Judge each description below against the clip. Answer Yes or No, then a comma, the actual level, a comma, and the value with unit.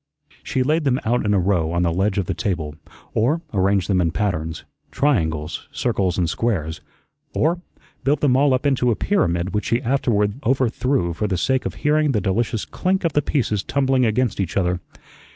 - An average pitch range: No, wide, 6.7 semitones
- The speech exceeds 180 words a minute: Yes, average, 190 wpm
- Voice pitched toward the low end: Yes, low, 105 Hz